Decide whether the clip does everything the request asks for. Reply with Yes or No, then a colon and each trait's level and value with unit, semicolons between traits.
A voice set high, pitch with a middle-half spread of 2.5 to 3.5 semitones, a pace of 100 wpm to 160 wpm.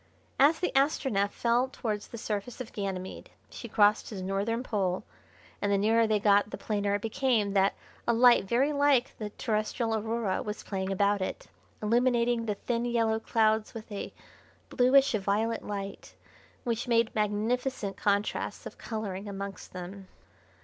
Yes: high, 215 Hz; average, 2.8 semitones; average, 155 wpm